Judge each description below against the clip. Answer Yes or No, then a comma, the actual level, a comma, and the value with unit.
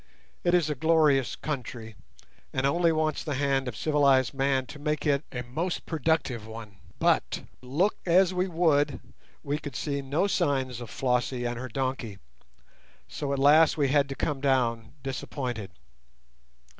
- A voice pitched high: No, medium, 140 Hz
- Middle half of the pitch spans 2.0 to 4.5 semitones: Yes, average, 3.5 semitones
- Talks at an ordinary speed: Yes, average, 155 wpm